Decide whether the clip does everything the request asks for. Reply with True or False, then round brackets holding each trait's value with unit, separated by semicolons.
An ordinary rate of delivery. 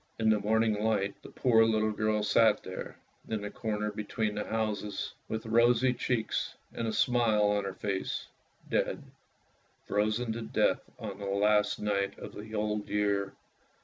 True (170 wpm)